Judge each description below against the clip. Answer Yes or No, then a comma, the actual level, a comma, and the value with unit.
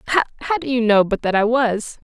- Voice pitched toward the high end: Yes, high, 235 Hz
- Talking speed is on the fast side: Yes, fast, 230 wpm